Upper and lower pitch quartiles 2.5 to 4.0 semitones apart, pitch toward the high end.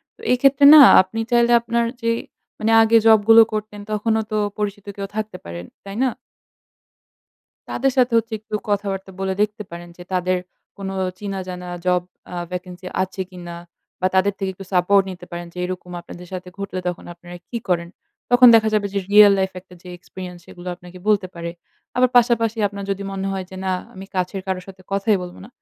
Yes: average, 2.9 semitones; high, 195 Hz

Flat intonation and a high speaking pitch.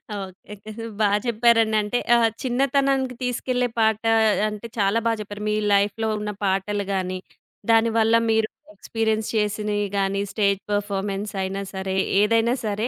Yes: narrow, 2.2 semitones; high, 210 Hz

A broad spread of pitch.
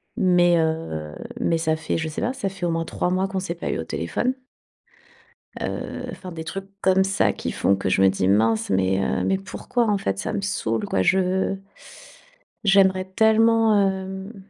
Yes: wide, 6.9 semitones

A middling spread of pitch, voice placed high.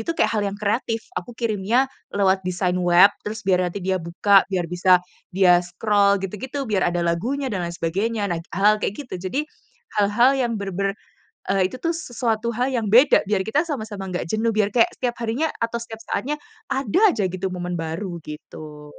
Yes: average, 4.1 semitones; high, 200 Hz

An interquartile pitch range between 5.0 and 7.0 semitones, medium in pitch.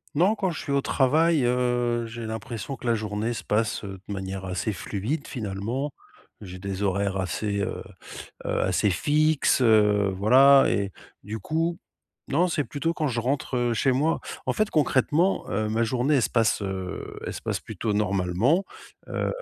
No: wide, 5.5 semitones; low, 115 Hz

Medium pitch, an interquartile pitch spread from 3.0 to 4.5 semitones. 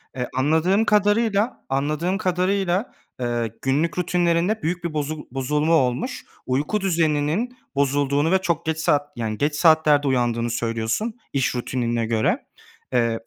No: medium, 150 Hz; wide, 5.6 semitones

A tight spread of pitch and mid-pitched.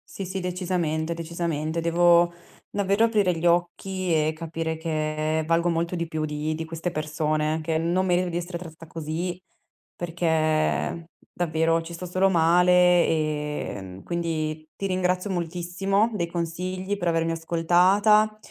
Yes: narrow, 2.2 semitones; medium, 170 Hz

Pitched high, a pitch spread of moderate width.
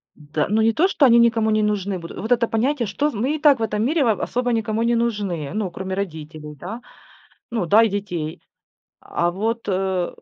Yes: high, 215 Hz; average, 3.9 semitones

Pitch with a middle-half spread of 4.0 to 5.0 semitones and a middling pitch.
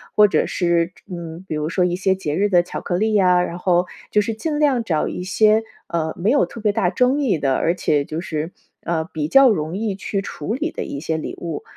Yes: average, 4.5 semitones; medium, 180 Hz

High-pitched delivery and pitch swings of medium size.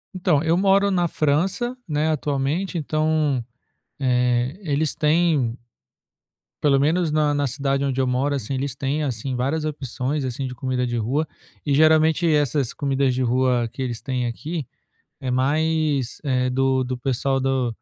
No: medium, 140 Hz; average, 3.2 semitones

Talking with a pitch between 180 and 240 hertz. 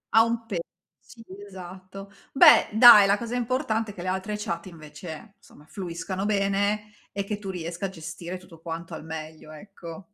Yes: high, 190 Hz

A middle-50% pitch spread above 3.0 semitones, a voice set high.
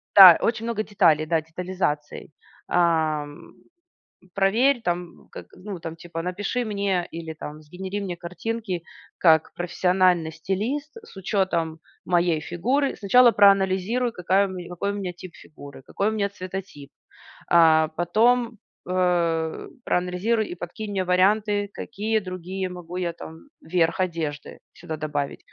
No: average, 3.5 semitones; medium, 180 Hz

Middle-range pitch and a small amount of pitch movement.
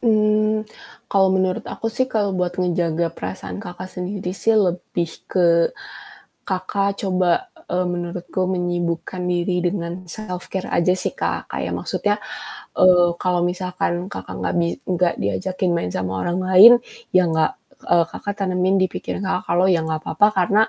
Yes: medium, 180 Hz; narrow, 1.5 semitones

